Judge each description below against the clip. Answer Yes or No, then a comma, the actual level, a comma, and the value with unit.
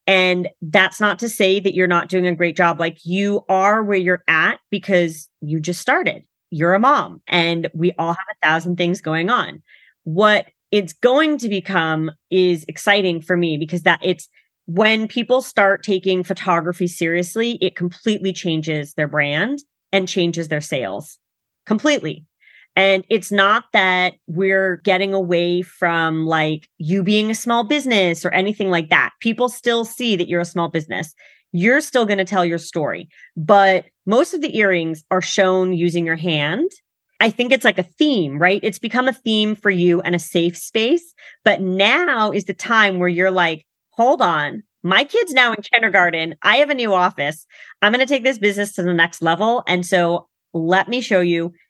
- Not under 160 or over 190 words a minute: Yes, average, 185 wpm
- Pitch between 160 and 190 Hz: Yes, medium, 185 Hz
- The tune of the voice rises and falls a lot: No, average, 3.8 semitones